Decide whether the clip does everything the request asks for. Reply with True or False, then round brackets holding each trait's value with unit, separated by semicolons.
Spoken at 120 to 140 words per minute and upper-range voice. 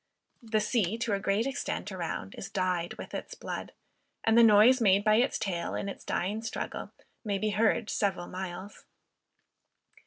False (165 wpm; 205 Hz)